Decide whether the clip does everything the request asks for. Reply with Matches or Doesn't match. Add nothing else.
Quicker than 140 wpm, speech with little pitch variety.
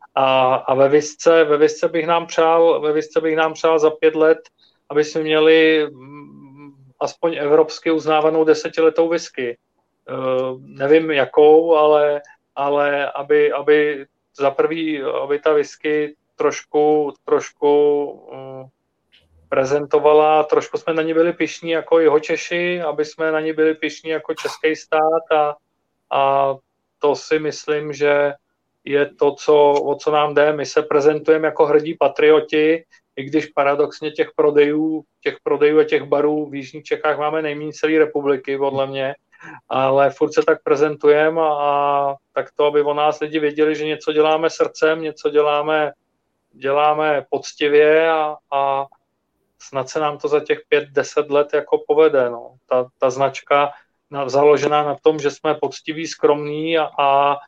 Matches